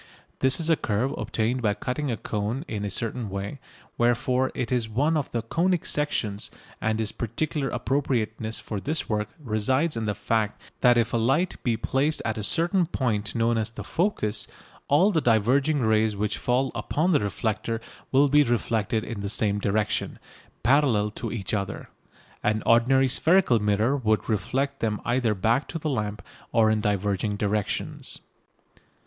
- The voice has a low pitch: Yes, low, 115 Hz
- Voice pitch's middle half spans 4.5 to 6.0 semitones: No, average, 4.1 semitones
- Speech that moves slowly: No, average, 170 wpm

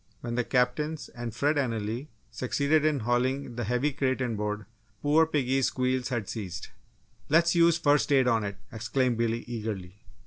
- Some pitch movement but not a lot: Yes, average, 3.8 semitones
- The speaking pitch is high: No, low, 125 Hz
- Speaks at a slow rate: No, average, 160 wpm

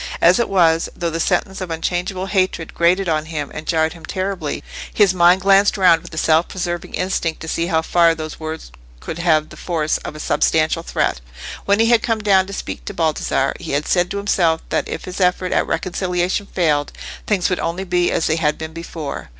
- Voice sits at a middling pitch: Yes, medium, 175 Hz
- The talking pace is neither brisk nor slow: No, fast, 215 wpm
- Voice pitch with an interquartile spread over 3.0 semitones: No, average, 2.7 semitones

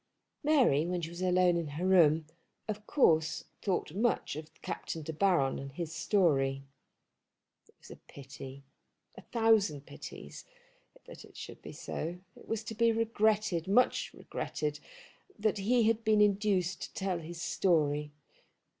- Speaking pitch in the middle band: Yes, medium, 180 Hz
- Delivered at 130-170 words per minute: Yes, average, 150 wpm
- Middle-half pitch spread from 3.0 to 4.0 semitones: No, wide, 5.5 semitones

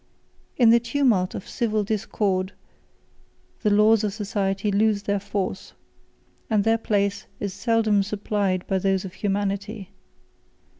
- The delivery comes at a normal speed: No, slow, 130 wpm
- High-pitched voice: Yes, high, 205 Hz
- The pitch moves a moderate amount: No, narrow, 1.9 semitones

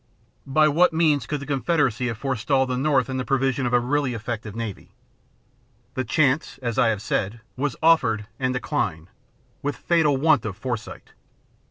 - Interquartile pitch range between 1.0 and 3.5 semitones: No, average, 4.0 semitones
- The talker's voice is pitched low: Yes, low, 130 Hz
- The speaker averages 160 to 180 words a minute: Yes, average, 170 wpm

